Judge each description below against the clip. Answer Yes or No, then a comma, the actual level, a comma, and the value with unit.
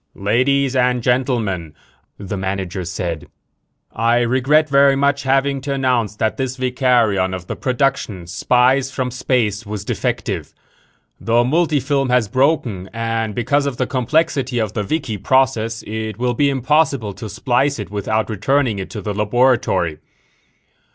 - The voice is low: Yes, low, 120 Hz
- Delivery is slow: No, average, 145 wpm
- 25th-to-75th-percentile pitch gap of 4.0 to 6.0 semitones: Yes, average, 4.3 semitones